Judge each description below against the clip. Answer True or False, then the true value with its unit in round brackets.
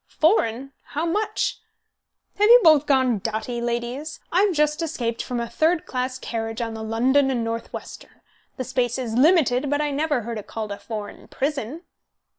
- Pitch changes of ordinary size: True (4.7 semitones)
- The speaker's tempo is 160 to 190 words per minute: True (170 wpm)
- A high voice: True (255 Hz)